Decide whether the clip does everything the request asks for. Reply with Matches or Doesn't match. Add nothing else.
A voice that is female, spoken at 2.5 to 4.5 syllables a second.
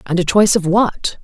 Doesn't match